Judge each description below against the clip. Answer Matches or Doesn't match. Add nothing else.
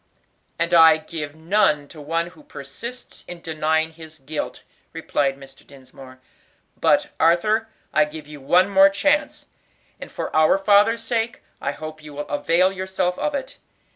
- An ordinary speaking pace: Matches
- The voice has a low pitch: Doesn't match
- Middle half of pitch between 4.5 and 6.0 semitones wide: Matches